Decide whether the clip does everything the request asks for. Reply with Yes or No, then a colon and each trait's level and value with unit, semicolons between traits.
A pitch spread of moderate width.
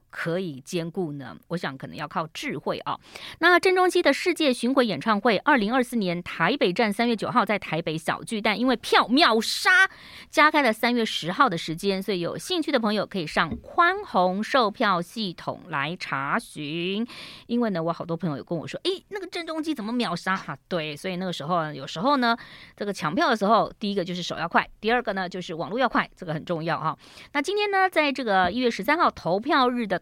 No: wide, 7.4 semitones